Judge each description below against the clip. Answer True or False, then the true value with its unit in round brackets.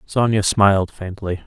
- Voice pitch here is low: True (100 Hz)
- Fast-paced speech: False (125 wpm)